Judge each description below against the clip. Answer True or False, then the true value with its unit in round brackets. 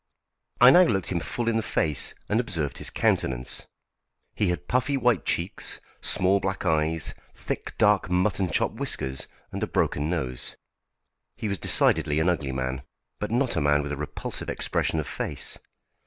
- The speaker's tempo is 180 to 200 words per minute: False (170 wpm)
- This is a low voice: True (90 Hz)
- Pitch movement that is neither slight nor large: False (6.2 semitones)